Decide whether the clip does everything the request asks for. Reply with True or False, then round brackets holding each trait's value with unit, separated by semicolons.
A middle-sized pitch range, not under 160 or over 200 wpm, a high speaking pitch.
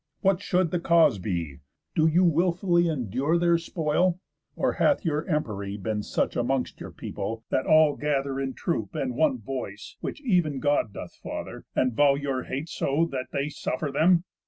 False (4.9 semitones; 175 wpm; 145 Hz)